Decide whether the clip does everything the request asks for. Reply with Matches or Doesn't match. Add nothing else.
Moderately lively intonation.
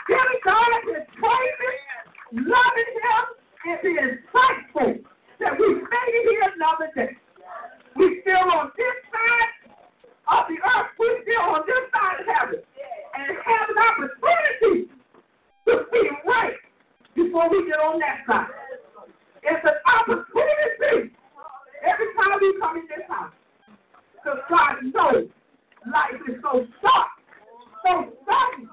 Doesn't match